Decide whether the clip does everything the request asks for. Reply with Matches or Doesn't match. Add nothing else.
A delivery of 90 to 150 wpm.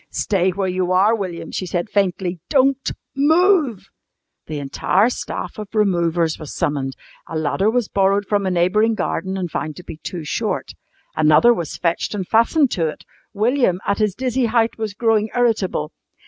Doesn't match